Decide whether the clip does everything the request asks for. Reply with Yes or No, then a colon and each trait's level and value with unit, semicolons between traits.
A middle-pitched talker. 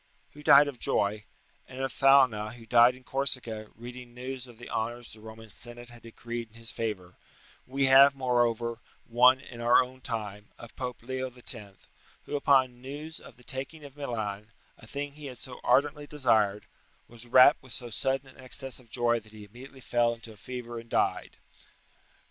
No: low, 125 Hz